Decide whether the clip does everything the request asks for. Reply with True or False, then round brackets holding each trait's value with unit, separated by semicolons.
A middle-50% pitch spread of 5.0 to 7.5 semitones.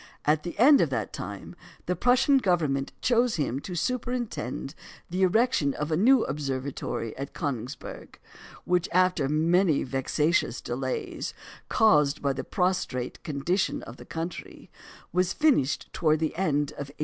True (5.3 semitones)